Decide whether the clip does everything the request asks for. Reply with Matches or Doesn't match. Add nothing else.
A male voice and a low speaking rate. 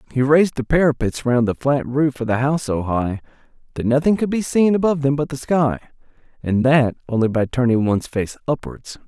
Doesn't match